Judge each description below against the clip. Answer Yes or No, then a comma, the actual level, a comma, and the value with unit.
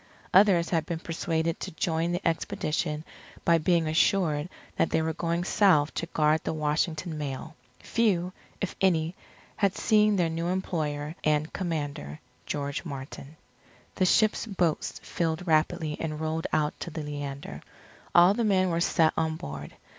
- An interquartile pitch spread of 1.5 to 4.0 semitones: Yes, average, 2.7 semitones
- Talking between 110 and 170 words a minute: Yes, average, 155 wpm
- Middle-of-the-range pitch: Yes, medium, 160 Hz